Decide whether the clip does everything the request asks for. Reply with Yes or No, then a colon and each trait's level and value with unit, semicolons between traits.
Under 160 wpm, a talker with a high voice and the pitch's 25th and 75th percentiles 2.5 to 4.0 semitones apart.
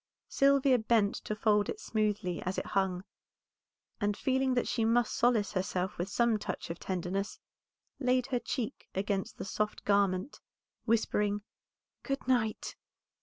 Yes: average, 140 wpm; high, 215 Hz; average, 3.7 semitones